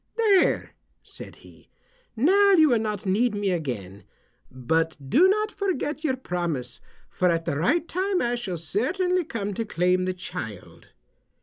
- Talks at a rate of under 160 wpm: Yes, average, 150 wpm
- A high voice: Yes, high, 210 Hz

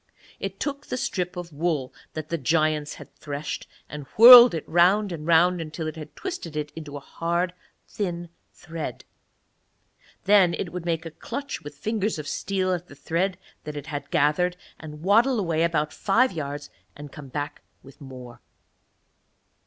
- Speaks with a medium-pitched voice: Yes, medium, 165 Hz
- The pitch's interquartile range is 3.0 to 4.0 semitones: Yes, average, 3.5 semitones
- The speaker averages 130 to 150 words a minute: No, average, 165 wpm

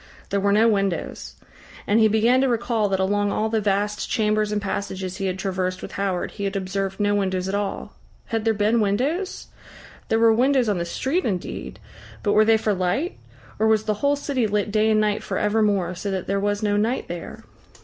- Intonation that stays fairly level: Yes, narrow, 2.1 semitones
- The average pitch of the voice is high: Yes, high, 210 Hz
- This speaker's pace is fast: Yes, fast, 210 wpm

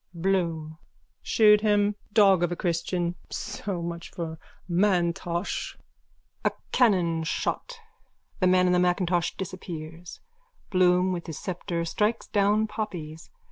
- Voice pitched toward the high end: No, medium, 180 Hz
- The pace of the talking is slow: Yes, slow, 115 wpm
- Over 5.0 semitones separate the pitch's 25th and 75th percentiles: No, average, 2.9 semitones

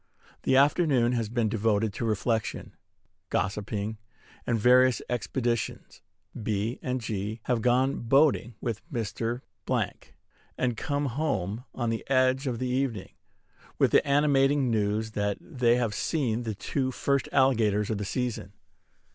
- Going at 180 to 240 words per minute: No, slow, 135 wpm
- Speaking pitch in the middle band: No, low, 120 Hz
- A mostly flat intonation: No, average, 3.2 semitones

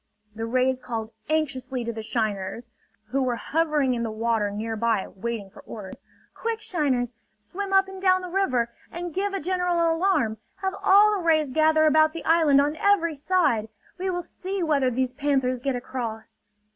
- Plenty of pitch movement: Yes, wide, 7.1 semitones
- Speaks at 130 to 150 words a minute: No, average, 175 wpm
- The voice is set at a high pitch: Yes, very high, 280 Hz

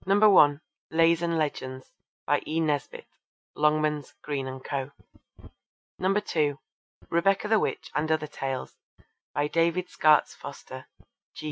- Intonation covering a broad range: No, narrow, 2.6 semitones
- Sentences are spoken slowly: Yes, slow, 115 wpm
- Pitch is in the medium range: Yes, medium, 155 Hz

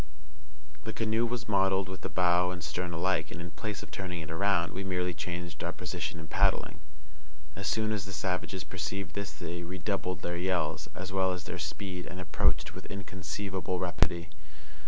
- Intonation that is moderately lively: No, narrow, 1.9 semitones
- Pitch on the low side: Yes, very low, 90 Hz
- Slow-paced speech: No, average, 180 wpm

